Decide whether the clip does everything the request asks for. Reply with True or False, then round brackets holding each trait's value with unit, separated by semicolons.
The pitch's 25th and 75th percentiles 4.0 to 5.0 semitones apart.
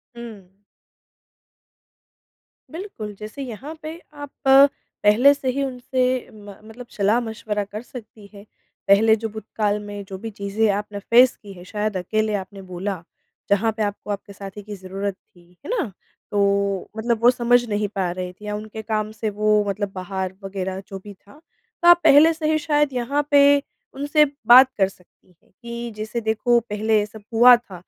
False (3.4 semitones)